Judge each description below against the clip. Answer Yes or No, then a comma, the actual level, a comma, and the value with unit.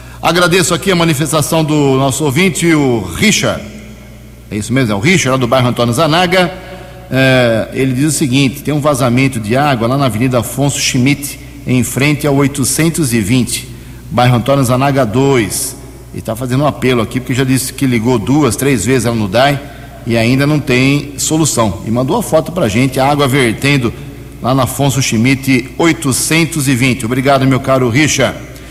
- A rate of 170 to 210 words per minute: Yes, average, 175 wpm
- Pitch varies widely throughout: No, average, 2.7 semitones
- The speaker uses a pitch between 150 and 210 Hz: No, low, 135 Hz